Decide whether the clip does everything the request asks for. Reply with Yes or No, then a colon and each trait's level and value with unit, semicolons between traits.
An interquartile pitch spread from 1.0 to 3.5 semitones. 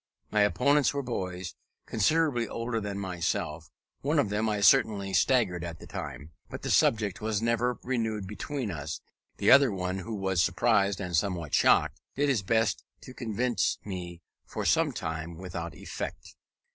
No: average, 4.6 semitones